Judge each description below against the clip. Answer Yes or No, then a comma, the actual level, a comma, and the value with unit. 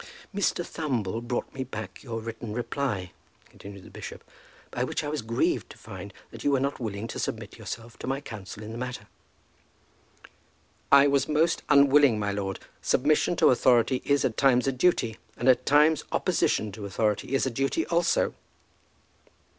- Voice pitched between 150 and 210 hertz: No, low, 125 Hz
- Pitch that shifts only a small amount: No, average, 4.2 semitones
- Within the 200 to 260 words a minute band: No, average, 170 wpm